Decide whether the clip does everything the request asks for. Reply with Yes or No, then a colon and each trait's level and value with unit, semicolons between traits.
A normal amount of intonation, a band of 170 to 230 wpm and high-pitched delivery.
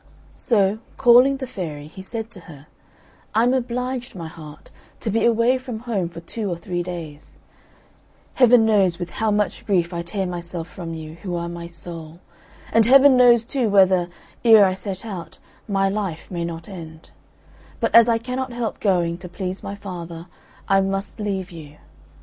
Yes: average, 5.0 semitones; average, 180 wpm; high, 195 Hz